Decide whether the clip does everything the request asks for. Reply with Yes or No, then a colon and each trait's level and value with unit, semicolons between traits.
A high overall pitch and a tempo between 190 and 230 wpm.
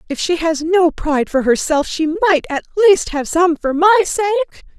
Yes: very high, 340 Hz; average, 200 wpm